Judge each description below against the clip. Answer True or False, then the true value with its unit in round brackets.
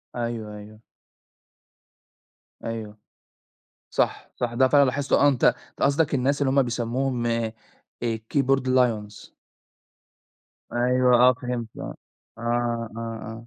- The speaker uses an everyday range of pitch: False (2.2 semitones)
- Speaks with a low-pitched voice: True (120 Hz)